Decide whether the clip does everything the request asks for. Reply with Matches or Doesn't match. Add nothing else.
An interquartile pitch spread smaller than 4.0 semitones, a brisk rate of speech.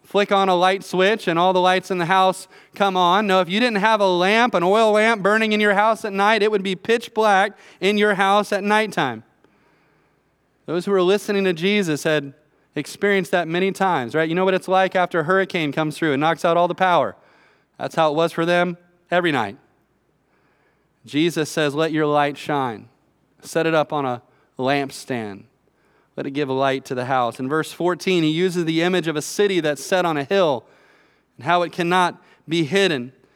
Doesn't match